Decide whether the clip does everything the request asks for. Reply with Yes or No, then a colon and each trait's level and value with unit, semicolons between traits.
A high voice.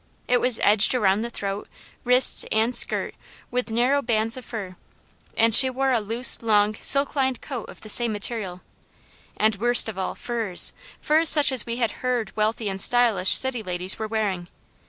Yes: high, 225 Hz